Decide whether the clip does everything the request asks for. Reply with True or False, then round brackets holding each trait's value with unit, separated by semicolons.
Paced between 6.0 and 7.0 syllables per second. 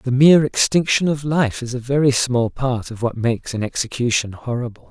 False (5.3 syllables/s)